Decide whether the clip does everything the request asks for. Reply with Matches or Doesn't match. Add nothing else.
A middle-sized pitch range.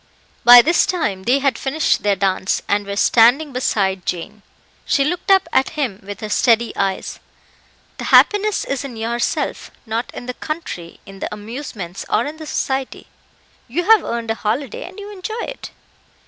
Doesn't match